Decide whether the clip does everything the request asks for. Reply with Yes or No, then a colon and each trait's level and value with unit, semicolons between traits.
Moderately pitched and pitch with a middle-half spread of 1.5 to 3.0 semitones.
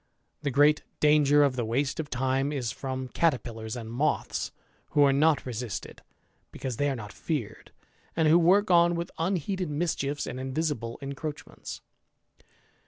No: medium, 145 Hz; average, 3.6 semitones